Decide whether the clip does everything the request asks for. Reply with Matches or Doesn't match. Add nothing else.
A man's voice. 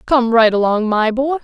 Doesn't match